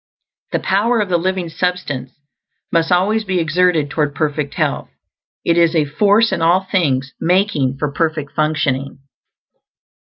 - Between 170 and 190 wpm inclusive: No, average, 145 wpm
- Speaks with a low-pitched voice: No, medium, 165 Hz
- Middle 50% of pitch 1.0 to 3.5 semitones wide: No, average, 4.0 semitones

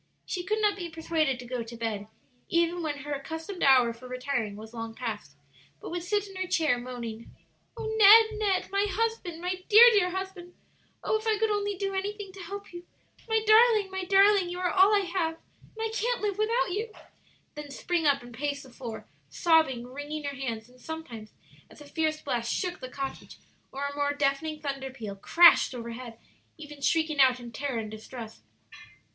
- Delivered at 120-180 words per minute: No, average, 200 wpm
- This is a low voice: No, very high, 320 Hz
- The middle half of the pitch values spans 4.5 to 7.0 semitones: No, wide, 7.4 semitones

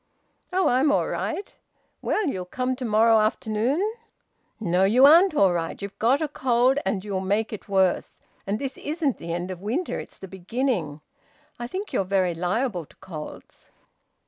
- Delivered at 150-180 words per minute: Yes, average, 170 wpm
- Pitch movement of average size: No, wide, 6.2 semitones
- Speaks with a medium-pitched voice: No, high, 220 Hz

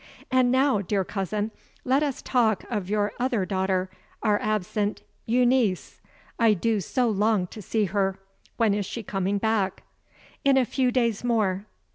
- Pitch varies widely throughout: No, average, 3.6 semitones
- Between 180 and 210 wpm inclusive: No, average, 155 wpm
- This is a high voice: Yes, high, 215 Hz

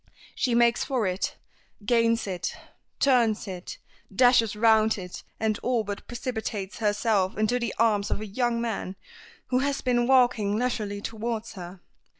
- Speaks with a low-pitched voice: No, high, 225 Hz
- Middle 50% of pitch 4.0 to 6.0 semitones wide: No, average, 2.9 semitones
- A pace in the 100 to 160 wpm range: Yes, average, 150 wpm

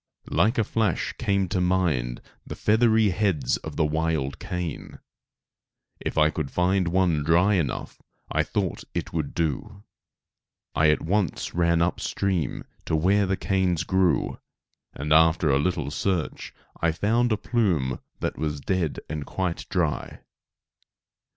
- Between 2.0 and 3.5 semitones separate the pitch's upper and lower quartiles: No, average, 3.9 semitones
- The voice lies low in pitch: Yes, very low, 85 Hz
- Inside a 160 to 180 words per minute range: No, average, 145 wpm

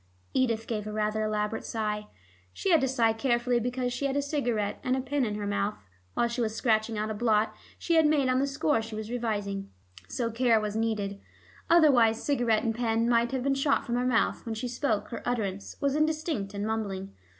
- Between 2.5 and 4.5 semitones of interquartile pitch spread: Yes, average, 3.3 semitones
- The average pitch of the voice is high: Yes, high, 230 Hz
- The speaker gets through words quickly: Yes, fast, 215 wpm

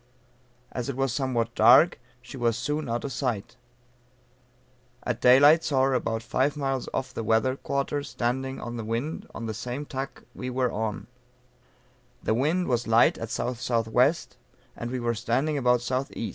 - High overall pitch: No, low, 125 Hz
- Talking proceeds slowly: No, average, 165 wpm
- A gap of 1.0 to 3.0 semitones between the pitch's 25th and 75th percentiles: Yes, narrow, 2.6 semitones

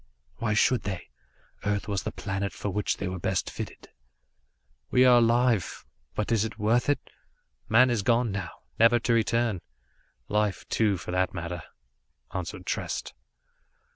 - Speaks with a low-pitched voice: Yes, low, 105 Hz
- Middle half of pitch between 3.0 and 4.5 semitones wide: Yes, average, 3.5 semitones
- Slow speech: No, average, 150 wpm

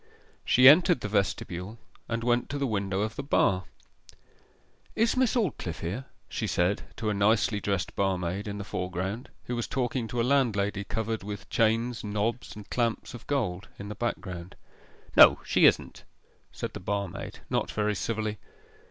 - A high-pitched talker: No, low, 105 Hz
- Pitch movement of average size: Yes, average, 3.4 semitones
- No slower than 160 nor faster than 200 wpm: Yes, average, 165 wpm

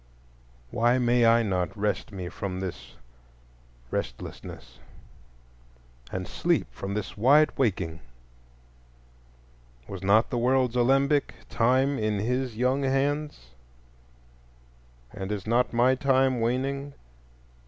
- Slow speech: Yes, slow, 105 wpm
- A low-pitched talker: Yes, low, 120 Hz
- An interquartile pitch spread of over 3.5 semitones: Yes, average, 5.0 semitones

